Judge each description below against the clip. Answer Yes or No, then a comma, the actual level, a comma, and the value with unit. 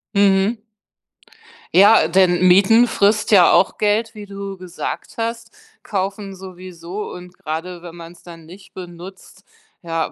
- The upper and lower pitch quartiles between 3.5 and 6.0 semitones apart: No, narrow, 2.5 semitones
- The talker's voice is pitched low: No, high, 190 Hz